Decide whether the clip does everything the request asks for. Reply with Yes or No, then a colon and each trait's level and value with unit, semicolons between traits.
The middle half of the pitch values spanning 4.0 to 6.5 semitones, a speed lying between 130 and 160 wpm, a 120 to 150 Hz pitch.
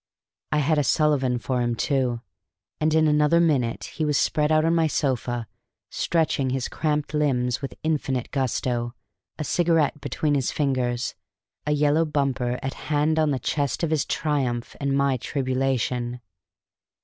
No: average, 3.4 semitones; average, 155 wpm; medium, 140 Hz